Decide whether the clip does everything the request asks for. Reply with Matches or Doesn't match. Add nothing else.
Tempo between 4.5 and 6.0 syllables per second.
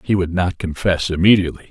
Doesn't match